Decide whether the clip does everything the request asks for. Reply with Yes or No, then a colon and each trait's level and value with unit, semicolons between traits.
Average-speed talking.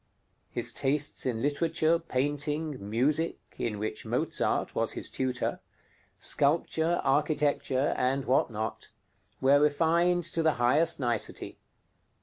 No: slow, 115 wpm